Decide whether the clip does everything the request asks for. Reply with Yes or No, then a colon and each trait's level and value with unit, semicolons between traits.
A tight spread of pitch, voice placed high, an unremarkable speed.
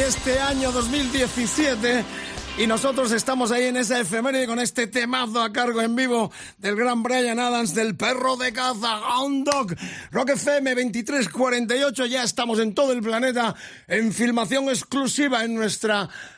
Yes: narrow, 2.1 semitones; high, 245 Hz; average, 150 wpm